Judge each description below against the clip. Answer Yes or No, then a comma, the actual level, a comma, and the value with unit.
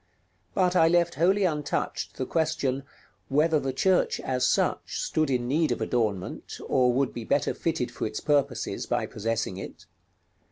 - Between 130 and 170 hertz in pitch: Yes, medium, 140 Hz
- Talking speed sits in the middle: Yes, average, 160 wpm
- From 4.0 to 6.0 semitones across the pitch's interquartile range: Yes, average, 4.7 semitones